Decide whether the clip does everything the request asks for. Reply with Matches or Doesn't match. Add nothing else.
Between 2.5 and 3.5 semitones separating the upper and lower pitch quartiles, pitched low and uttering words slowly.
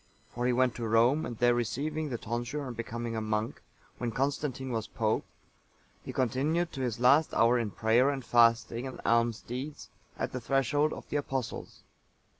Doesn't match